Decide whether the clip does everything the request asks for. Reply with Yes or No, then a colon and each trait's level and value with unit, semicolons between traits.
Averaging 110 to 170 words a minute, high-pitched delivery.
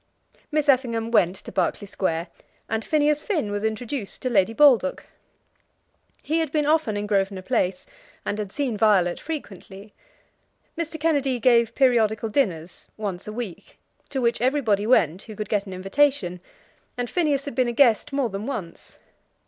Yes: average, 160 wpm; high, 225 Hz